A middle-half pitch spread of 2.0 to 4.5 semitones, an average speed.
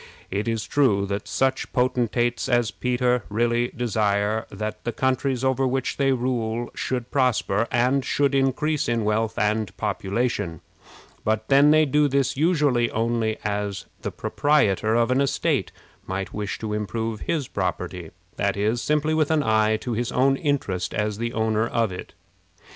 Yes: average, 3.7 semitones; average, 160 wpm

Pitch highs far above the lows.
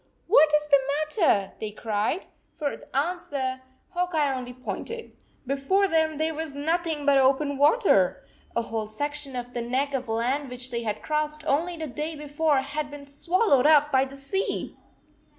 No: average, 3.2 semitones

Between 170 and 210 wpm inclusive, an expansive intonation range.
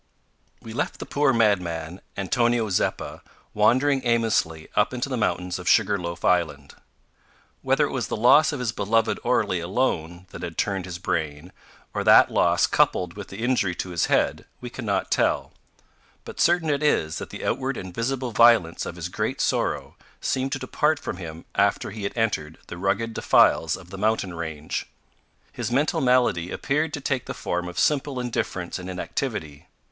Yes: average, 175 wpm; wide, 6.0 semitones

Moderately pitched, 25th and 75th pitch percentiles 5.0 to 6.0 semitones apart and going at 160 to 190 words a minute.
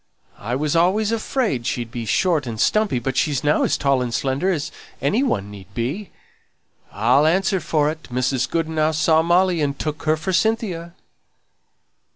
Yes: medium, 155 Hz; wide, 5.6 semitones; average, 165 wpm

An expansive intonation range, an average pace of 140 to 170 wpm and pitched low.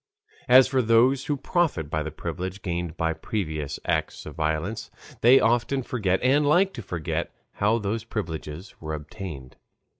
Yes: wide, 7.5 semitones; average, 155 wpm; low, 100 Hz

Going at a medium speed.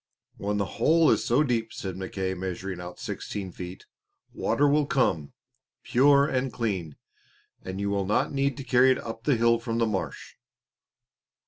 Yes: average, 165 wpm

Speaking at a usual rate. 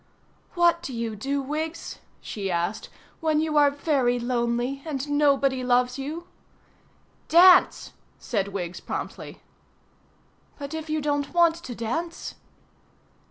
No: slow, 120 wpm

